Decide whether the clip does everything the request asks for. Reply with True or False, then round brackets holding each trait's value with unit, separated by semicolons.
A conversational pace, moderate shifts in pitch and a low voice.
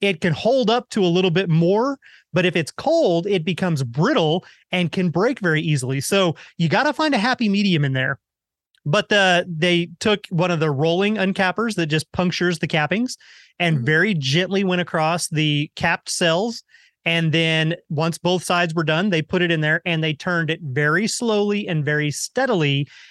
False (190 wpm; 3.6 semitones; 175 Hz)